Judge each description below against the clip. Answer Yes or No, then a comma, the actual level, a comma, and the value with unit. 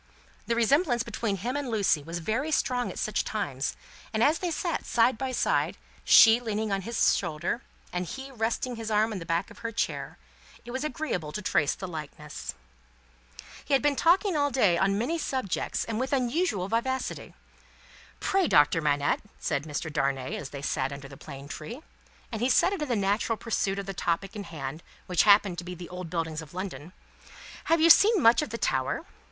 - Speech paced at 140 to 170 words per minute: No, average, 200 wpm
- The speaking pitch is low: No, high, 215 Hz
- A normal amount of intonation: No, wide, 7.2 semitones